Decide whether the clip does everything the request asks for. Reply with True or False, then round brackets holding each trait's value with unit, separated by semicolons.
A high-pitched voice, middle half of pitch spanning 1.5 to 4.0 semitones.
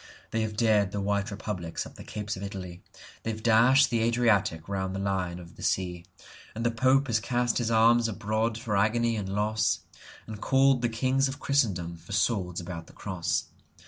False (110 Hz; 3.6 semitones)